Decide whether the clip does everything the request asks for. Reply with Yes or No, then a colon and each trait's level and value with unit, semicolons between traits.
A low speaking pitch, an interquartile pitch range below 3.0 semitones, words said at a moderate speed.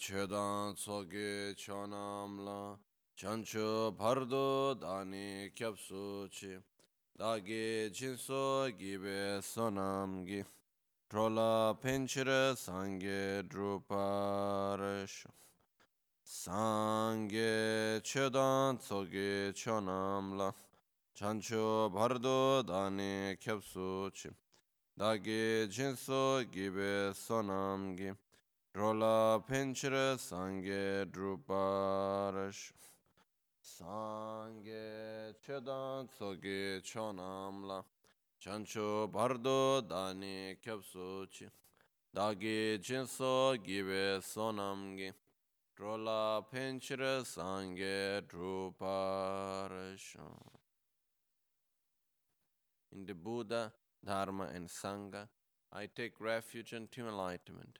No: low, 100 Hz; narrow, 2.4 semitones; slow, 60 wpm